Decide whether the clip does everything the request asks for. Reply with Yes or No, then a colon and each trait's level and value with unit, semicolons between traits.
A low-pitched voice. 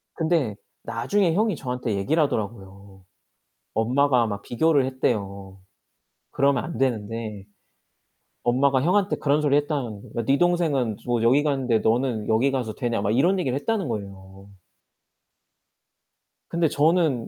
Yes: low, 125 Hz